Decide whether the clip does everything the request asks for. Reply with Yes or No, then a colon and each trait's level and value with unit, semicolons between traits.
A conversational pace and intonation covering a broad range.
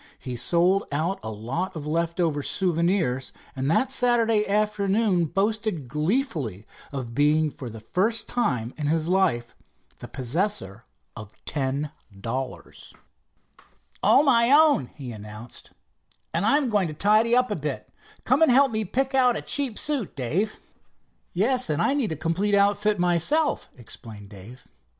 Yes: average, 145 wpm; wide, 8.4 semitones